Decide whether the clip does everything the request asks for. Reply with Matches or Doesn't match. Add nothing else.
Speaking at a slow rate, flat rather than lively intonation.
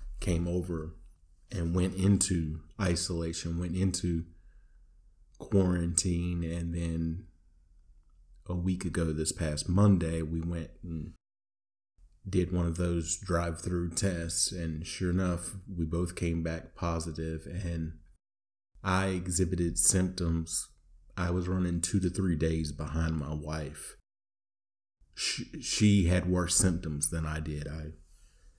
Matches